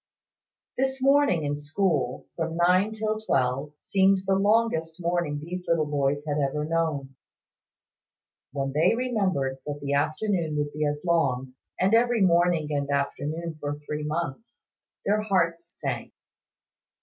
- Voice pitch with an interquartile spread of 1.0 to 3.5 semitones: No, average, 4.7 semitones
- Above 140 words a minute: No, slow, 135 wpm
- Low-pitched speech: No, medium, 160 Hz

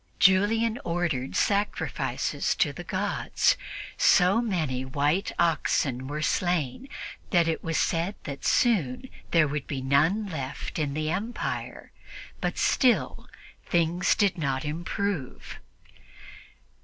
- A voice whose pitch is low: No, medium, 165 Hz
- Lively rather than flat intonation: Yes, wide, 5.7 semitones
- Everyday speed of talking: No, slow, 115 wpm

